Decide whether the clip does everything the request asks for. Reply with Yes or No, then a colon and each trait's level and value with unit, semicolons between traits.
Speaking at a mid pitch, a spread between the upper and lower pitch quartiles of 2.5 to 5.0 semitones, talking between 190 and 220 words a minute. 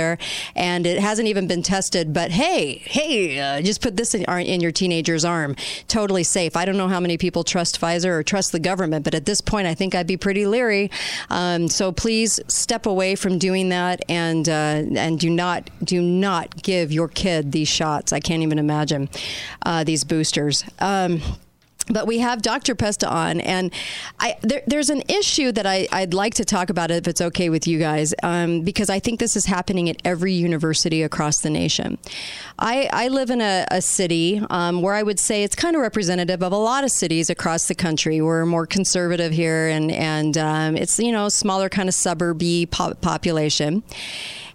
Yes: medium, 180 Hz; average, 3.3 semitones; average, 200 wpm